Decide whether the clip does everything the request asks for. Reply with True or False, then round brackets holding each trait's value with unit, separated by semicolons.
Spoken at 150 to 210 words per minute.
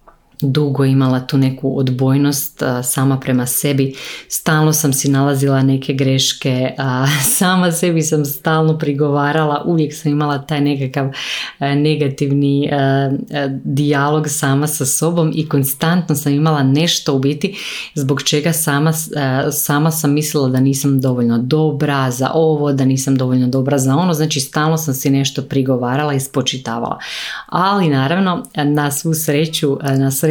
False (135 wpm)